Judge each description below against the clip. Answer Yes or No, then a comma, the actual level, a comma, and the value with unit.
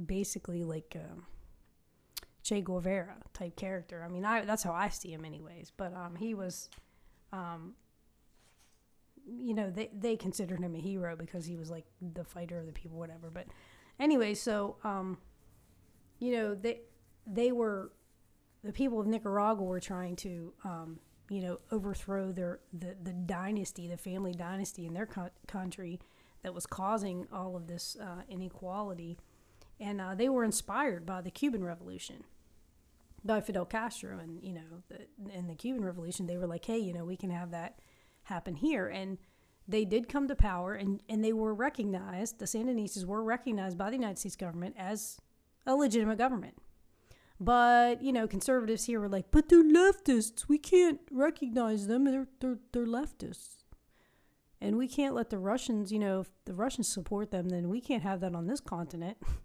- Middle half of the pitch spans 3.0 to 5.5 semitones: Yes, average, 4.2 semitones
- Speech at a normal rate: Yes, average, 175 wpm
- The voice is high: Yes, high, 195 Hz